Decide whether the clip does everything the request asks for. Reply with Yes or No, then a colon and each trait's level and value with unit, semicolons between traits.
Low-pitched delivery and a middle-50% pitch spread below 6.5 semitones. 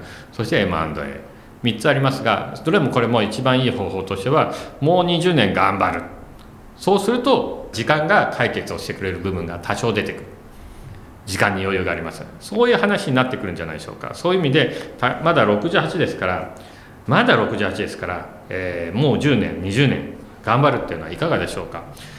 No: low, 115 Hz; wide, 7.5 semitones